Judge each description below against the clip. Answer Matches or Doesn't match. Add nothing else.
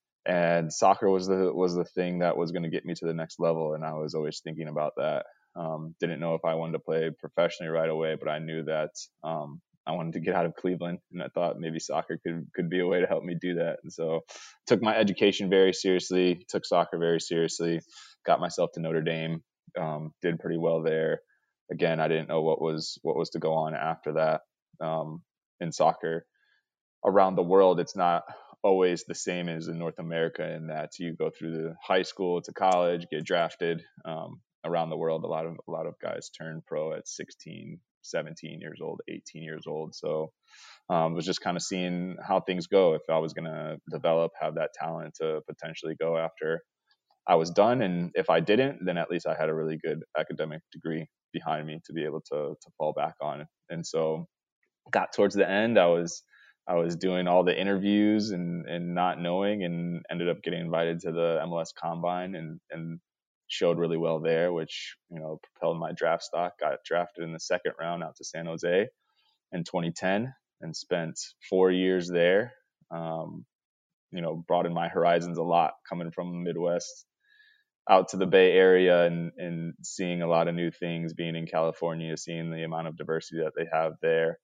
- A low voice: Matches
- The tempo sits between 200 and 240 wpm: Matches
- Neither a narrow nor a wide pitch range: Doesn't match